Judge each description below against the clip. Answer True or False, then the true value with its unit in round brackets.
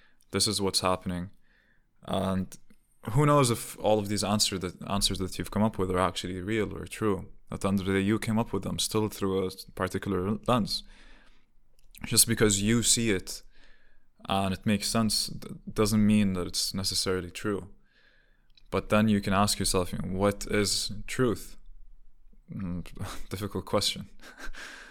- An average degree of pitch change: False (2.2 semitones)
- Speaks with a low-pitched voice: True (100 Hz)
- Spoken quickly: False (165 wpm)